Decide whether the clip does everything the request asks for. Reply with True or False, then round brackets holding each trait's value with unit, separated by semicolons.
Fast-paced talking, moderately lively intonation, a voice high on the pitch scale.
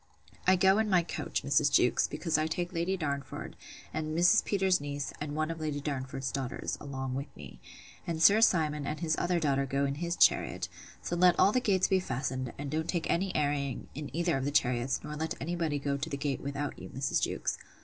False (220 wpm; 3.7 semitones; 150 Hz)